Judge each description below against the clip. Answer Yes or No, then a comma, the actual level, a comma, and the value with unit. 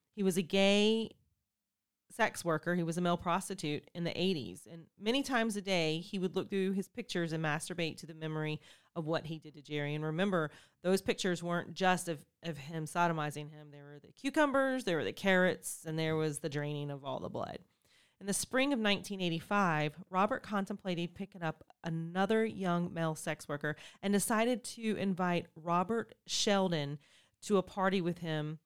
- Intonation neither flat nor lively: Yes, average, 3.7 semitones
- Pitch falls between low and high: Yes, medium, 175 Hz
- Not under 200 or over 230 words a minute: No, average, 185 wpm